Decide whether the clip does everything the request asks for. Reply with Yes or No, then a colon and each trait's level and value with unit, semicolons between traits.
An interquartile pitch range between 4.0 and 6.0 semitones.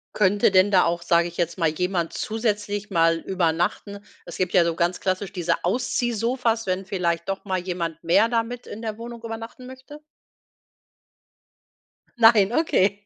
Yes: average, 4.6 semitones